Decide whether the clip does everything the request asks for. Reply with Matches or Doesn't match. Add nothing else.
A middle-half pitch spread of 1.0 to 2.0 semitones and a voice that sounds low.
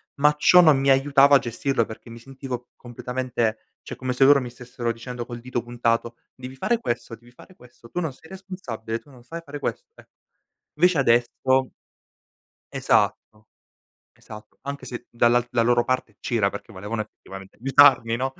Doesn't match